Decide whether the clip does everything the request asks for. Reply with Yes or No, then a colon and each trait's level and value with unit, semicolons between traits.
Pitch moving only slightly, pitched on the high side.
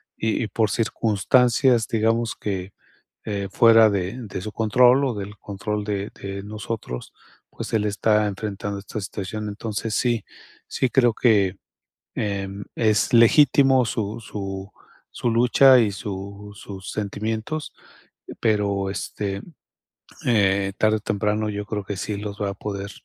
No: narrow, 2.1 semitones; low, 105 Hz